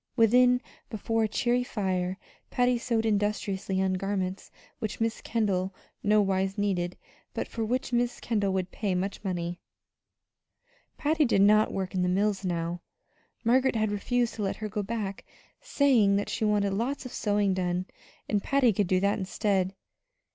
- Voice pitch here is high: Yes, high, 205 Hz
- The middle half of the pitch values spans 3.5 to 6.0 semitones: No, average, 3.1 semitones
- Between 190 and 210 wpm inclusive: No, average, 160 wpm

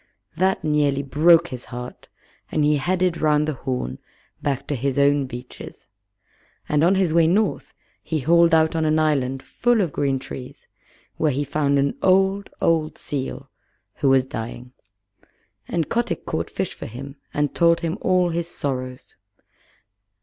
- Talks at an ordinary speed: Yes, average, 155 wpm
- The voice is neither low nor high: Yes, medium, 150 Hz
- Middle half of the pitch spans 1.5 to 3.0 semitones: No, average, 3.9 semitones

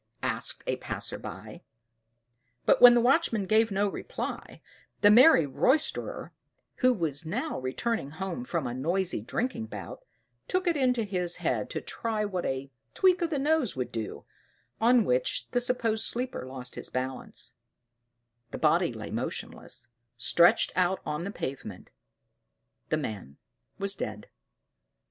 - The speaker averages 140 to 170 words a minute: Yes, average, 145 wpm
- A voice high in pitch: Yes, high, 200 Hz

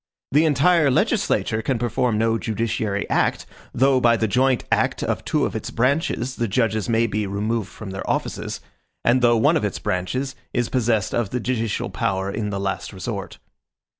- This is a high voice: No, low, 115 Hz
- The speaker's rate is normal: Yes, average, 180 wpm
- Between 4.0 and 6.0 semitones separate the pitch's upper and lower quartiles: No, average, 3.3 semitones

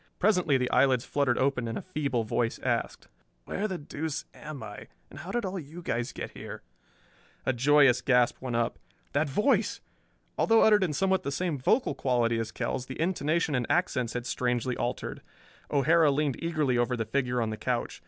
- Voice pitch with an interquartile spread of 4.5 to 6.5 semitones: Yes, average, 5.2 semitones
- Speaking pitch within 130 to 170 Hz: Yes, medium, 140 Hz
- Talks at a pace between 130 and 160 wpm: No, average, 185 wpm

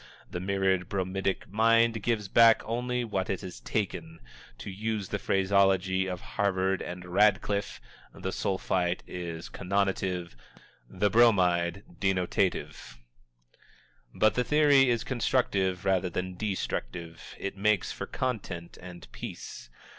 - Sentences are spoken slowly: Yes, slow, 120 wpm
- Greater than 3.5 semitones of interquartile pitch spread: No, average, 3.0 semitones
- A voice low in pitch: Yes, very low, 95 Hz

